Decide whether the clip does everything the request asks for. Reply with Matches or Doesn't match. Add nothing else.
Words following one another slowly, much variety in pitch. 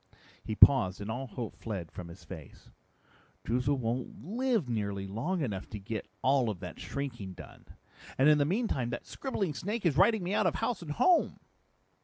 Doesn't match